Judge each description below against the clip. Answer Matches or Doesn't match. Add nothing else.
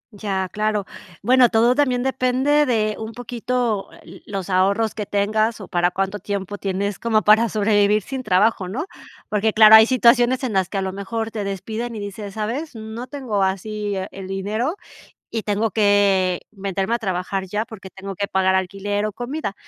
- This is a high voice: Matches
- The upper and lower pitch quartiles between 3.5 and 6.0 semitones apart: Doesn't match